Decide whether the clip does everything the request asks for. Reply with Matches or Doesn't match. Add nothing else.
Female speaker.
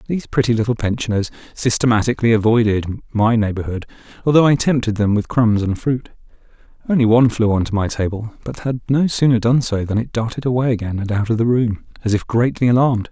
Doesn't match